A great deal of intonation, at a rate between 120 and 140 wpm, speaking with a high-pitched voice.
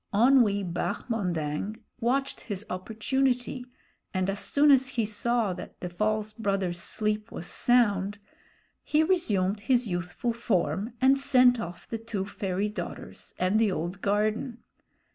No: average, 4.2 semitones; slow, 135 wpm; high, 215 Hz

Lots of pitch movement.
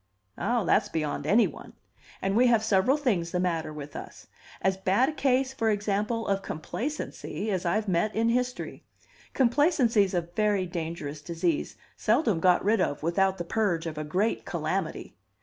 No: average, 5.0 semitones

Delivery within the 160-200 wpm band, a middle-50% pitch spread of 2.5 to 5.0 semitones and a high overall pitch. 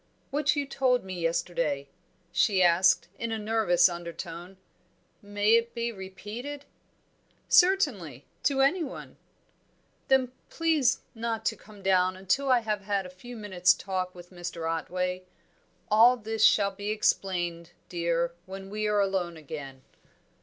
No: slow, 135 wpm; average, 4.7 semitones; high, 195 Hz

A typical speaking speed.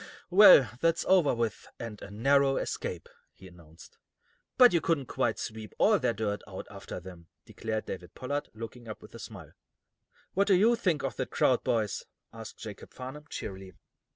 Yes: average, 175 wpm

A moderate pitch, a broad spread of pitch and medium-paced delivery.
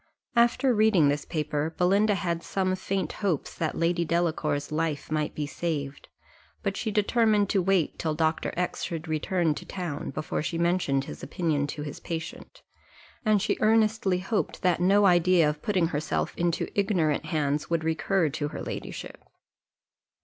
No: medium, 170 Hz; average, 4.0 semitones; average, 160 wpm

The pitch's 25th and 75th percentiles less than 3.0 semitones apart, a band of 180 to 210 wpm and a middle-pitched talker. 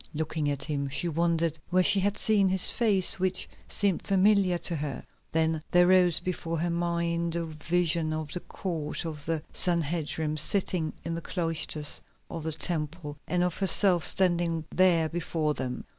No: narrow, 2.4 semitones; average, 165 wpm; medium, 170 Hz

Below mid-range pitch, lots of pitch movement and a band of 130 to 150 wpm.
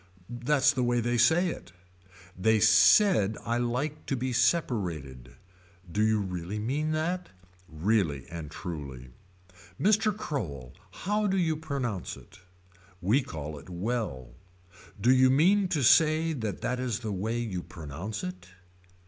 Yes: low, 115 Hz; wide, 8.3 semitones; average, 140 wpm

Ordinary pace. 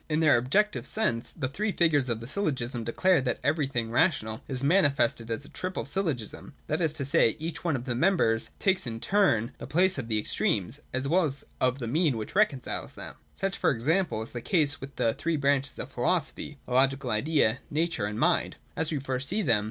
No: fast, 210 wpm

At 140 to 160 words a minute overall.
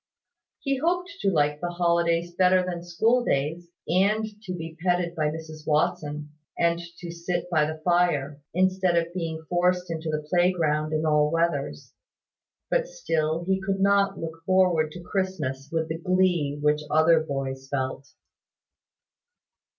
Yes: average, 150 wpm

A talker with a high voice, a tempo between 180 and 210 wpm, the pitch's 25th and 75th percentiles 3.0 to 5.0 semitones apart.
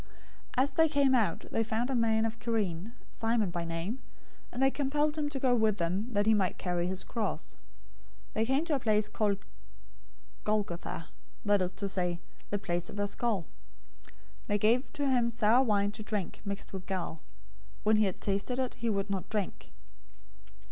Yes: high, 215 Hz; average, 190 wpm; average, 3.7 semitones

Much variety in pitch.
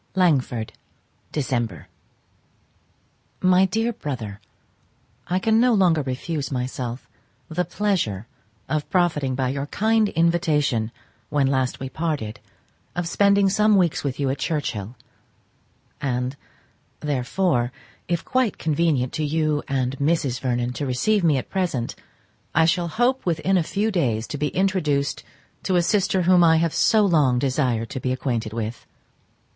Yes: wide, 6.0 semitones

